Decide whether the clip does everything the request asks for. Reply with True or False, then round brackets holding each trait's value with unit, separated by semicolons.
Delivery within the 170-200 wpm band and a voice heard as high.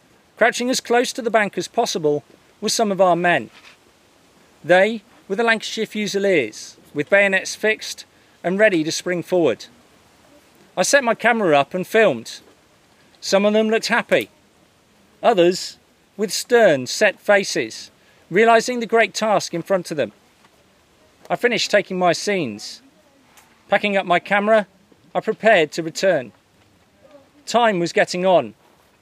False (140 wpm; 205 Hz)